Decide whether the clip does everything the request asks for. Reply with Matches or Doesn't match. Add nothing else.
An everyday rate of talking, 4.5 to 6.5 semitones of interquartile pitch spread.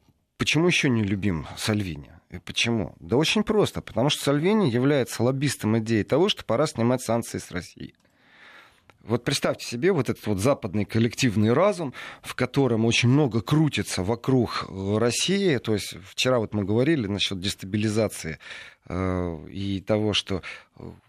Matches